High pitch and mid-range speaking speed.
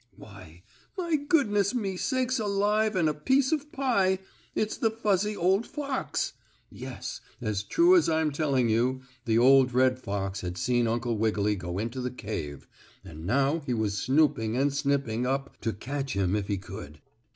No: low, 135 Hz; average, 170 wpm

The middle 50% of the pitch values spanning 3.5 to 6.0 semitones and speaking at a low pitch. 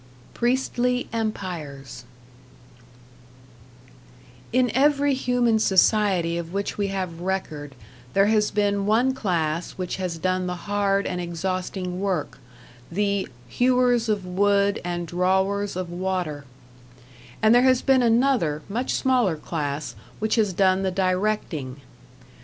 No: average, 3.9 semitones; high, 195 Hz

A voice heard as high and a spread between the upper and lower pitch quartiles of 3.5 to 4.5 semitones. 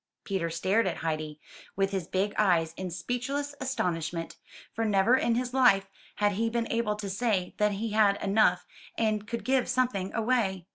Yes: high, 210 Hz; average, 3.8 semitones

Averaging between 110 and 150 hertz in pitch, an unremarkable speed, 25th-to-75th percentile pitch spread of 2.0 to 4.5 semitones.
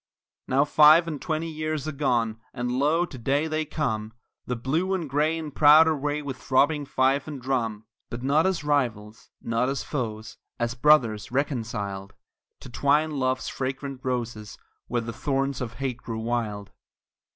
Yes: low, 135 Hz; average, 160 wpm; average, 4.2 semitones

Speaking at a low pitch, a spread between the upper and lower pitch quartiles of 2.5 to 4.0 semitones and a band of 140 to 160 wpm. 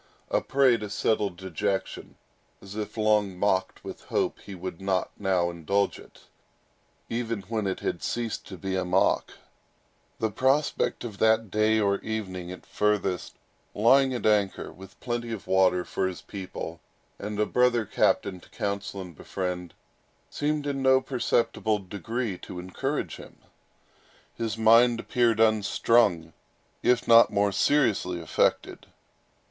Yes: low, 105 Hz; average, 3.5 semitones; average, 145 wpm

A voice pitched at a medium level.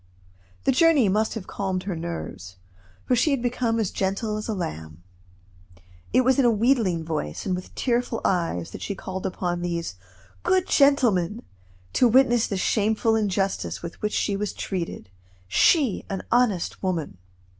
No: high, 205 Hz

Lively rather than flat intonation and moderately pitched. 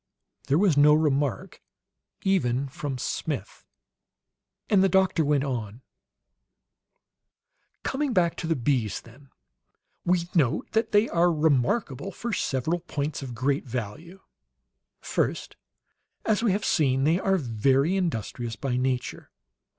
Yes: wide, 5.9 semitones; medium, 145 Hz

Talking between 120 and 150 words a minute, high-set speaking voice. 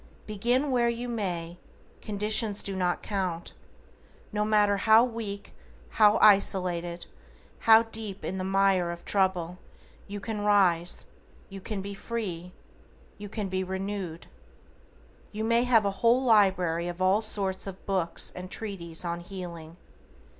Yes: average, 140 wpm; high, 195 Hz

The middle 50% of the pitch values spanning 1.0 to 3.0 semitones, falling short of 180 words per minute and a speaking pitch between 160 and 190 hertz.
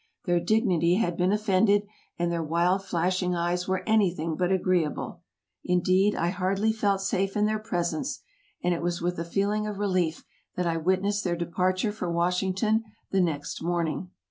Yes: narrow, 2.6 semitones; average, 170 wpm; medium, 185 Hz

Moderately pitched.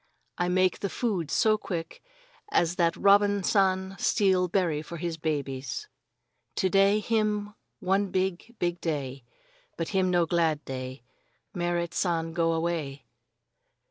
Yes: medium, 175 Hz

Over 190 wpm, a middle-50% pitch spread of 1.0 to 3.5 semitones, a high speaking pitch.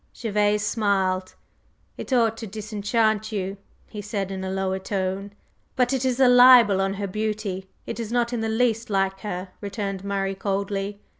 No: average, 170 wpm; narrow, 2.4 semitones; high, 205 Hz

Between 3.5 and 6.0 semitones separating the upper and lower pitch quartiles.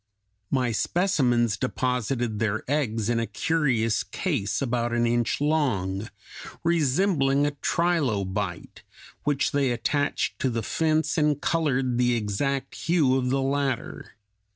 Yes: average, 4.1 semitones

